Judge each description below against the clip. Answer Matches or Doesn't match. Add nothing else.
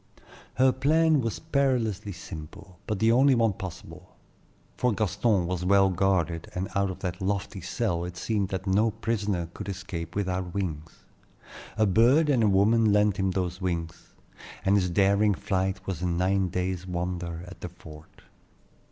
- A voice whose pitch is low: Matches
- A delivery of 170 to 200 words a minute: Doesn't match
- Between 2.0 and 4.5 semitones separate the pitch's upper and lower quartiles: Matches